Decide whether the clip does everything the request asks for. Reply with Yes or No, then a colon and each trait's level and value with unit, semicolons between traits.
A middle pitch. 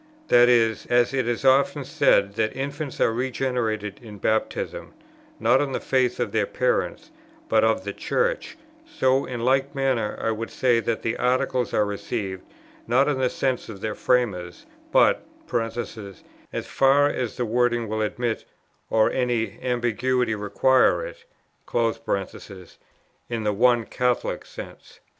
No: low, 120 Hz